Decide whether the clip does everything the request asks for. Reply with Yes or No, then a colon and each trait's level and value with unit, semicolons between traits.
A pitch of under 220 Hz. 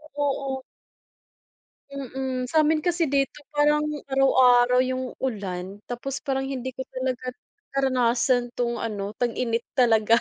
No: very high, 255 Hz